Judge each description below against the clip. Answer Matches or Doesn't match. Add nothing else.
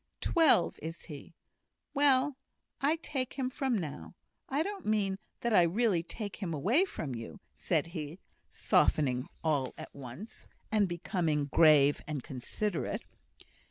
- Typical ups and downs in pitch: Doesn't match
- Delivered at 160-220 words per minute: Doesn't match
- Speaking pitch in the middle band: Matches